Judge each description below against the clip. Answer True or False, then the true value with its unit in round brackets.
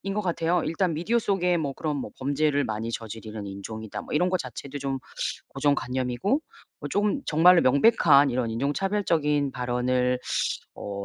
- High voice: False (140 Hz)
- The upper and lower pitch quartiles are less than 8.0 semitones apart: True (5.5 semitones)